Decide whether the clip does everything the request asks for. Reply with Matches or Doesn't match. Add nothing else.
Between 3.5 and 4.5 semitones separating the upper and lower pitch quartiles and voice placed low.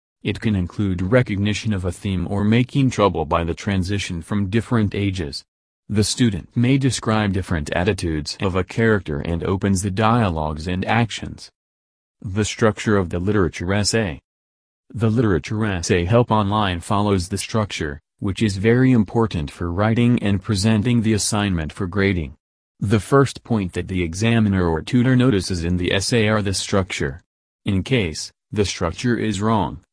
Matches